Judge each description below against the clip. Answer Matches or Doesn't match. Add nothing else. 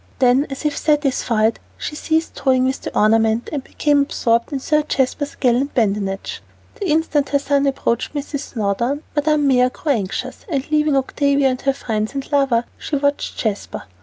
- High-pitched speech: Matches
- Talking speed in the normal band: Matches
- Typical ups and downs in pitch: Matches